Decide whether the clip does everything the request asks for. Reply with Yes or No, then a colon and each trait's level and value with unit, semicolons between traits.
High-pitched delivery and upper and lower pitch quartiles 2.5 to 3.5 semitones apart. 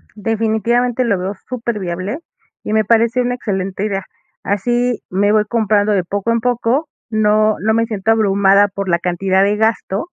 Yes: high, 215 Hz; average, 2.8 semitones